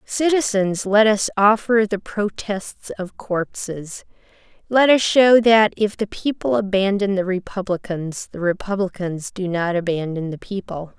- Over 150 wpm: No, slow, 135 wpm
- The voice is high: Yes, high, 195 Hz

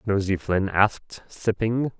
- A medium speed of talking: No, slow, 120 wpm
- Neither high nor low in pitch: No, low, 105 Hz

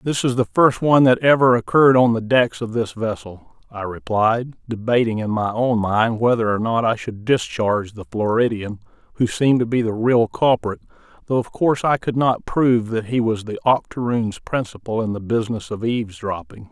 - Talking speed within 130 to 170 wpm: No, average, 195 wpm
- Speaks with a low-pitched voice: Yes, low, 115 Hz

